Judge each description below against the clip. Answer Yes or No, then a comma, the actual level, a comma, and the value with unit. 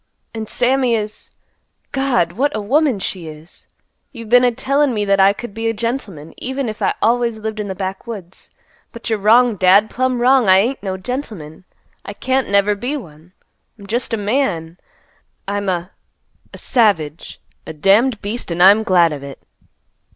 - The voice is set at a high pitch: Yes, high, 215 Hz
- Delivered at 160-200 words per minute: Yes, average, 170 wpm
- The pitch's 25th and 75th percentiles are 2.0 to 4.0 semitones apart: No, average, 4.5 semitones